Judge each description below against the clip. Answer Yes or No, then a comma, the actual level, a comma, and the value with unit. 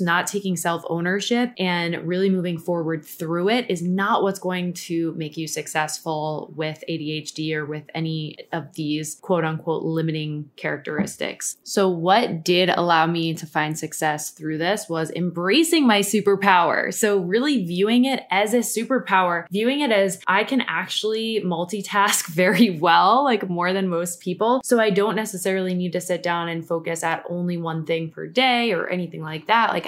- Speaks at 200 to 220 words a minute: No, average, 170 wpm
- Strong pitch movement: No, average, 3.8 semitones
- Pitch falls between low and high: Yes, medium, 175 Hz